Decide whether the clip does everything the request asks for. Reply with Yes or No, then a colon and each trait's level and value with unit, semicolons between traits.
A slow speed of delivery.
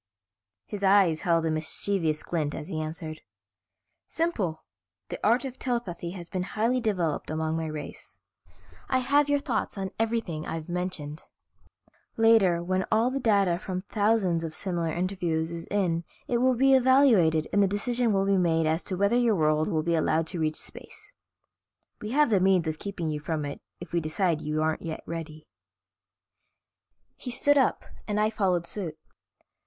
No: average, 170 wpm